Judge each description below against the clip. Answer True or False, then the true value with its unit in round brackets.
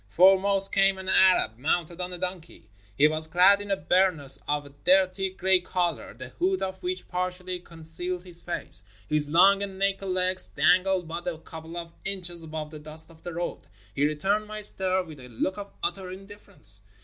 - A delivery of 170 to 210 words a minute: True (195 wpm)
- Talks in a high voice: False (180 Hz)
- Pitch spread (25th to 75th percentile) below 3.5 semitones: True (3.0 semitones)